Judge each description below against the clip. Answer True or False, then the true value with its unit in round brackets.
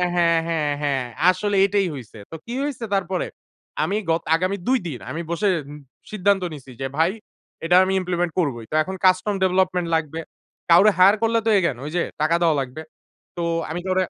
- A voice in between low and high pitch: True (175 Hz)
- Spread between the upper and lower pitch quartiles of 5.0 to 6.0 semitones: False (3.1 semitones)